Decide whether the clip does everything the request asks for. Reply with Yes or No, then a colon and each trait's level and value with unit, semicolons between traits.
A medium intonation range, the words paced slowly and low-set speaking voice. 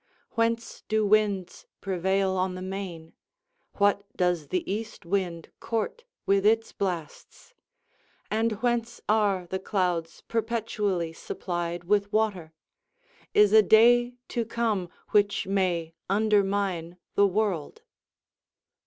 No: average, 3.3 semitones; slow, 110 wpm; high, 200 Hz